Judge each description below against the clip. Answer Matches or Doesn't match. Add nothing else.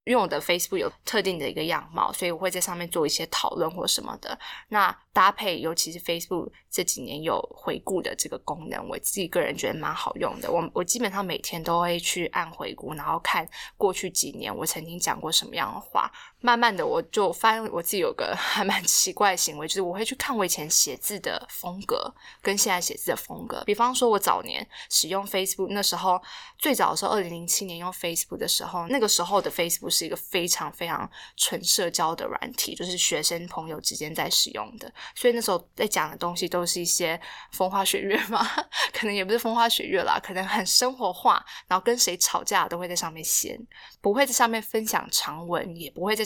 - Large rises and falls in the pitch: Doesn't match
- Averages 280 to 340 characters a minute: Doesn't match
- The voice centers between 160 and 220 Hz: Matches